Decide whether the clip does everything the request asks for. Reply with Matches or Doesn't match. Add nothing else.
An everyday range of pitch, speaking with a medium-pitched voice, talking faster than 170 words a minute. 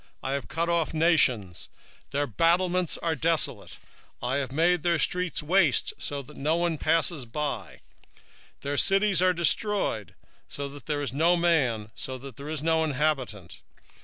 Doesn't match